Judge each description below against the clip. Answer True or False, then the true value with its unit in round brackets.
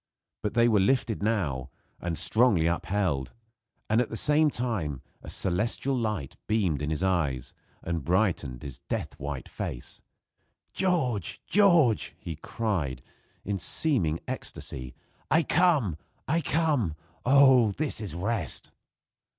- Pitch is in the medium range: False (105 Hz)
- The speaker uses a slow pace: True (125 wpm)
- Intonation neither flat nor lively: False (7.9 semitones)